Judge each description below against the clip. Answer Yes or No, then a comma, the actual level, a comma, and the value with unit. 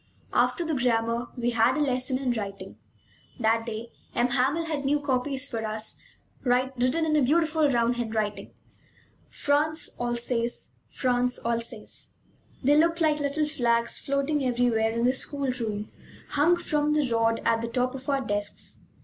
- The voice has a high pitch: Yes, very high, 250 Hz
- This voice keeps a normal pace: Yes, average, 155 wpm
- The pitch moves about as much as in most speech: Yes, average, 3.7 semitones